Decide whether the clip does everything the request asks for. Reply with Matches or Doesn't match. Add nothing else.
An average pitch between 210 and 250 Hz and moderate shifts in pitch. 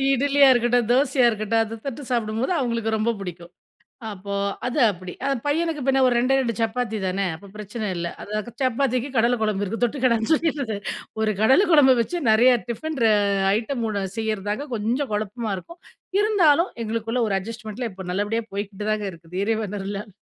Matches